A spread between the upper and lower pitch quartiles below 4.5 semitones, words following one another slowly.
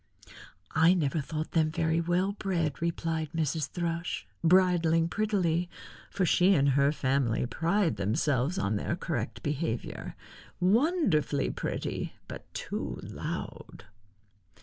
Yes: average, 3.6 semitones; slow, 115 wpm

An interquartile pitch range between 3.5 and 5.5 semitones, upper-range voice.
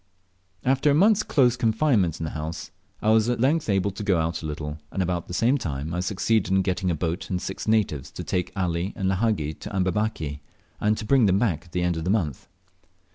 No: average, 4.9 semitones; very low, 95 Hz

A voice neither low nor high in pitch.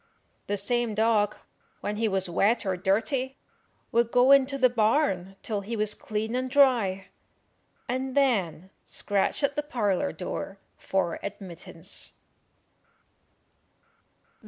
No: high, 215 Hz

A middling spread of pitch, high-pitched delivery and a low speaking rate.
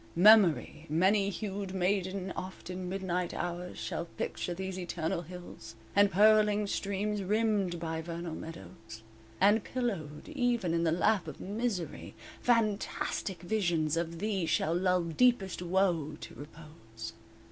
No: average, 3.5 semitones; medium, 180 Hz; slow, 130 wpm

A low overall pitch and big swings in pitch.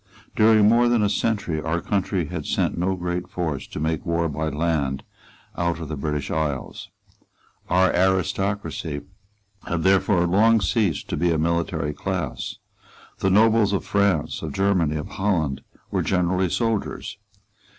No: very low, 90 Hz; average, 3.9 semitones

